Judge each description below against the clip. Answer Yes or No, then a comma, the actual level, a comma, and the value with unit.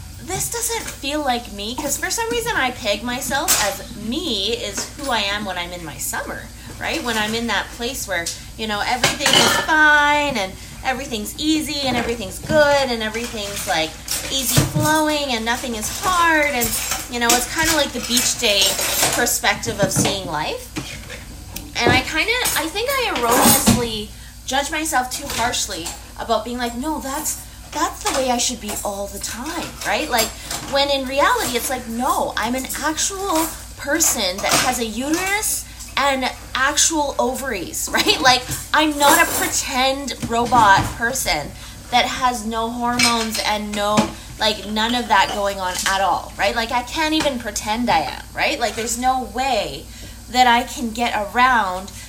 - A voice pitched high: Yes, very high, 250 Hz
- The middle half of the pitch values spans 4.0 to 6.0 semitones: Yes, average, 4.7 semitones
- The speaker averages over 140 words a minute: Yes, average, 170 wpm